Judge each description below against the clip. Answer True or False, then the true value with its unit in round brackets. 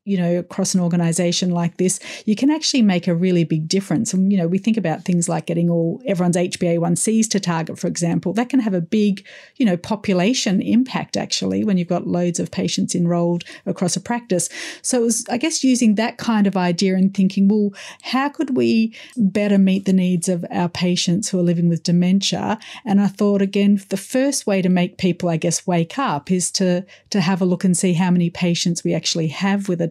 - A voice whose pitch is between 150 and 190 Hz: True (185 Hz)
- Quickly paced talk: True (220 wpm)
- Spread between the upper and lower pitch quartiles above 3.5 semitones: False (3.0 semitones)